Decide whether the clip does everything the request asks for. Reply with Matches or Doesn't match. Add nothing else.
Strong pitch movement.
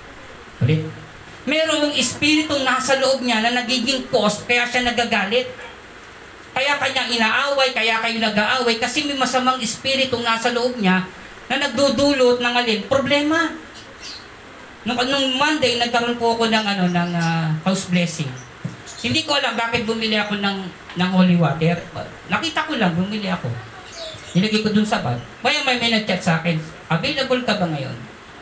Matches